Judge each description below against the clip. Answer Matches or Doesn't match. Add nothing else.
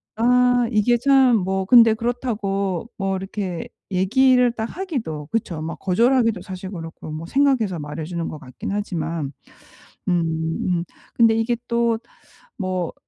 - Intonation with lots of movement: Doesn't match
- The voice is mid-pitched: Doesn't match